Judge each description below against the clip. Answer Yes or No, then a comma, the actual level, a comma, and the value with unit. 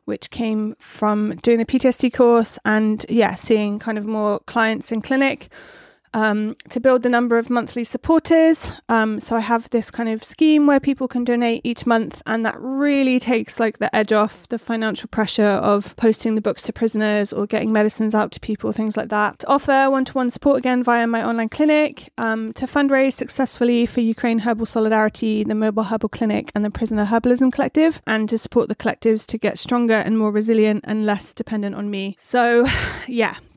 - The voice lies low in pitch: No, high, 230 Hz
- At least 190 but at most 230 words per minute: Yes, average, 195 wpm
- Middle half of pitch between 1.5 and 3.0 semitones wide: Yes, narrow, 2.5 semitones